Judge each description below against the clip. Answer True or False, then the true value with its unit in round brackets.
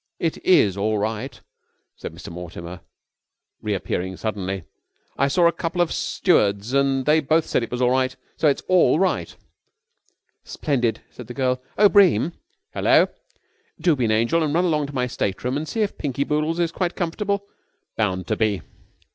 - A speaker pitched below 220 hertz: True (135 Hz)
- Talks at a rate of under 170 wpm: False (175 wpm)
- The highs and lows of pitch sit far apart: True (7.3 semitones)